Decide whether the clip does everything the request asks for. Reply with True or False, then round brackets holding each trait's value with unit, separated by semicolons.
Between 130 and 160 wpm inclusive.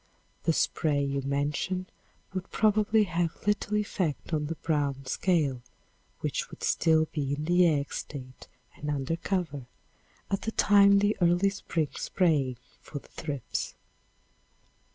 True (135 wpm)